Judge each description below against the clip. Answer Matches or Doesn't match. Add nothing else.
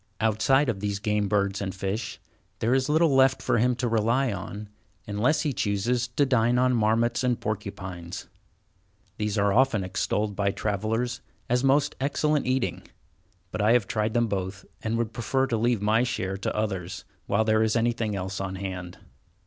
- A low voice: Matches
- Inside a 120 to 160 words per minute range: Doesn't match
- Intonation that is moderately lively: Matches